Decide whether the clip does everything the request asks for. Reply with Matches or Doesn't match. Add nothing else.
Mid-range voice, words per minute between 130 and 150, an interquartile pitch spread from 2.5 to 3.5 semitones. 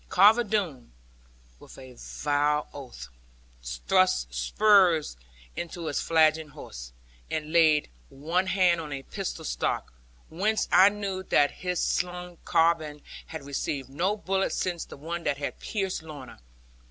Doesn't match